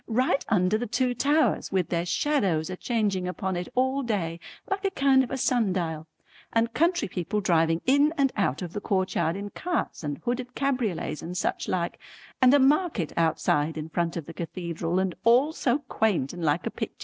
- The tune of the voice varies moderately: No, wide, 7.2 semitones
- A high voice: Yes, high, 200 Hz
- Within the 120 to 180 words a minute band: No, average, 195 wpm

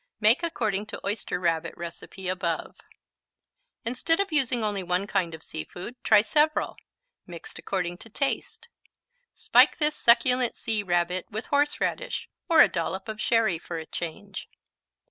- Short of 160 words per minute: Yes, average, 145 wpm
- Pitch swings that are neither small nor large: No, wide, 5.9 semitones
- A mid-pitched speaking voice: No, high, 205 Hz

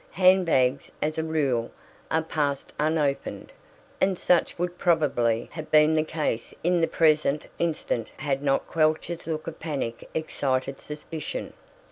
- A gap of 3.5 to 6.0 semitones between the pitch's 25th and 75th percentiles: No, average, 2.9 semitones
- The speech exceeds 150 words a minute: No, average, 140 wpm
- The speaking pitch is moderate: Yes, medium, 155 Hz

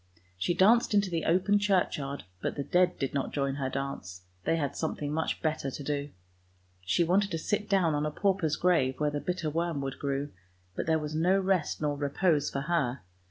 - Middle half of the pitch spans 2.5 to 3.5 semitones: No, average, 4.2 semitones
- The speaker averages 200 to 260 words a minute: Yes, fast, 205 wpm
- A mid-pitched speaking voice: Yes, medium, 155 Hz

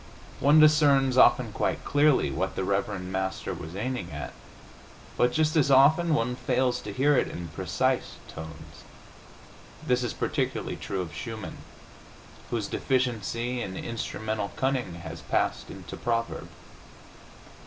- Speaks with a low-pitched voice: Yes, low, 120 Hz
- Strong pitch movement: Yes, wide, 5.8 semitones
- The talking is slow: Yes, slow, 130 wpm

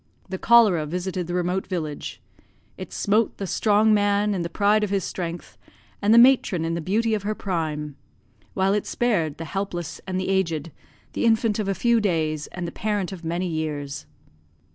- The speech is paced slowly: No, average, 185 wpm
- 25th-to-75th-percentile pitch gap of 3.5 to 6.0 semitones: Yes, average, 3.9 semitones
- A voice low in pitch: No, high, 190 Hz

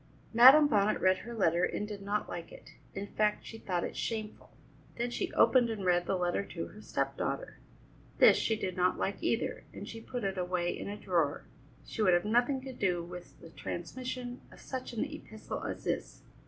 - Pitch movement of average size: Yes, average, 4.8 semitones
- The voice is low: No, high, 210 Hz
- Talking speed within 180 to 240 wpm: Yes, fast, 205 wpm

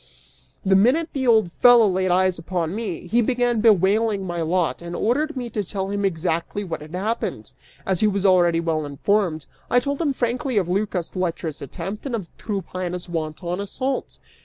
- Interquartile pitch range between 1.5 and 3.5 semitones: No, average, 4.7 semitones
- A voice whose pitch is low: No, high, 190 Hz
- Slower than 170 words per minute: No, average, 180 wpm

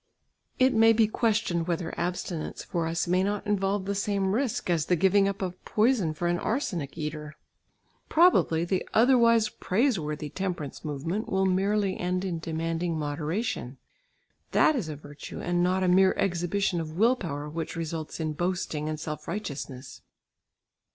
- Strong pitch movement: No, average, 4.1 semitones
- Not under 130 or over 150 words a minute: No, average, 160 wpm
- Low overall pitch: No, medium, 180 Hz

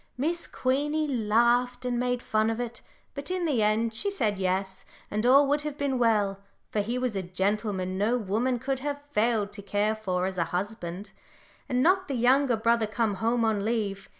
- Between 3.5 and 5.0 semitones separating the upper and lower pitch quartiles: Yes, average, 3.9 semitones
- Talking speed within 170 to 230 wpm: Yes, average, 195 wpm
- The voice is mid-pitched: No, high, 230 Hz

